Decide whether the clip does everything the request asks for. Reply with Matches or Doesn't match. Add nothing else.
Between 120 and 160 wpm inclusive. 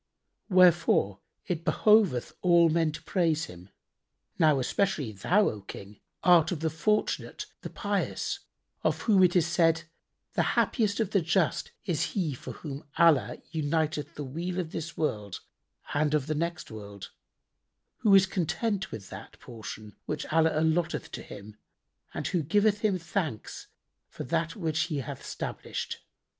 Matches